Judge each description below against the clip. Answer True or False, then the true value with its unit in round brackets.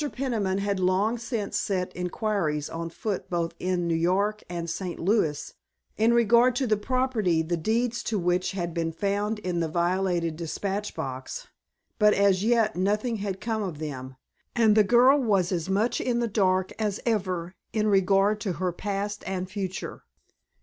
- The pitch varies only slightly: False (3.5 semitones)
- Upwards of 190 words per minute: False (170 wpm)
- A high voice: True (195 Hz)